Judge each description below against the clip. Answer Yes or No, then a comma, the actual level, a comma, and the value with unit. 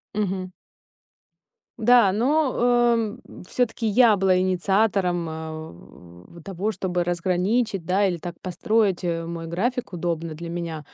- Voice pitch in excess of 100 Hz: Yes, medium, 185 Hz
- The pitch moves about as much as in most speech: Yes, average, 3.8 semitones